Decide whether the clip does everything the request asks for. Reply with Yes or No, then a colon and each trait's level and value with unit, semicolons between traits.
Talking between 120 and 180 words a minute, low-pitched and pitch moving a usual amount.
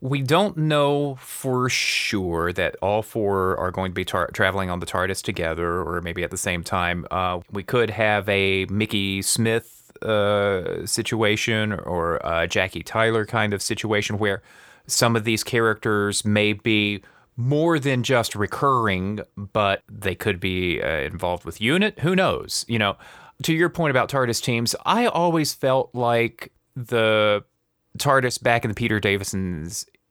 Yes: average, 160 wpm; low, 105 Hz; average, 4.1 semitones